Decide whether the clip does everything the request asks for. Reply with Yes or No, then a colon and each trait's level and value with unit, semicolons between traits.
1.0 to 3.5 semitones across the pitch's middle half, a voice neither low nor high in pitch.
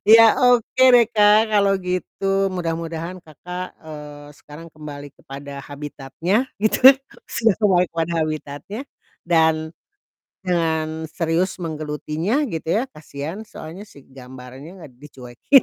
No: average, 4.7 semitones; medium, 165 Hz